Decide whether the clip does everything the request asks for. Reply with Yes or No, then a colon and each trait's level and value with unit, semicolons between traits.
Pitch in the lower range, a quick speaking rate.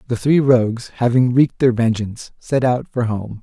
No: low, 120 Hz; average, 195 wpm